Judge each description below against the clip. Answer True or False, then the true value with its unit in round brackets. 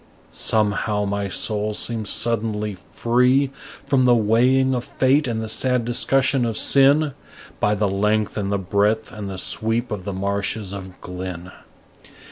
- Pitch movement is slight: False (3.6 semitones)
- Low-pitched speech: True (110 Hz)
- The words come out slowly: False (150 wpm)